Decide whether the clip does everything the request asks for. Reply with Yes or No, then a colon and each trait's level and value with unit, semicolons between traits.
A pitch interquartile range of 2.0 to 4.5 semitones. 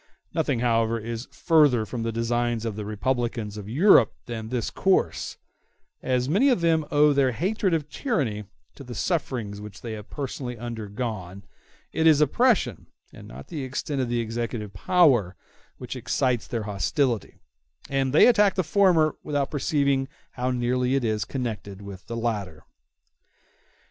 No: average, 4.9 semitones